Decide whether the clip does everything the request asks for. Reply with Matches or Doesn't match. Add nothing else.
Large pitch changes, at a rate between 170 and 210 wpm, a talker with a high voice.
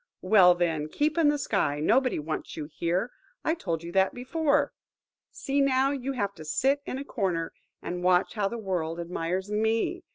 Matches